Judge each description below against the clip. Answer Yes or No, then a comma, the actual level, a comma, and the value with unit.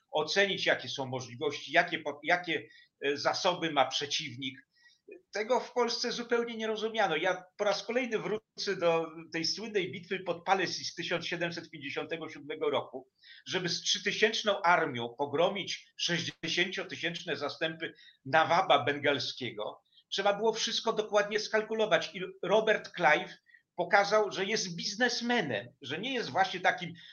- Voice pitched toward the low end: No, medium, 180 Hz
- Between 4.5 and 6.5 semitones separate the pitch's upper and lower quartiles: Yes, average, 5.1 semitones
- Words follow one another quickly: No, average, 125 wpm